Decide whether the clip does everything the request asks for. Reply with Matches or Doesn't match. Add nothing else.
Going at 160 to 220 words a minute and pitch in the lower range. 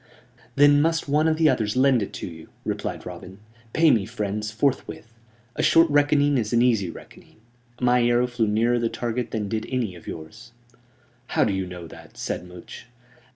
Matches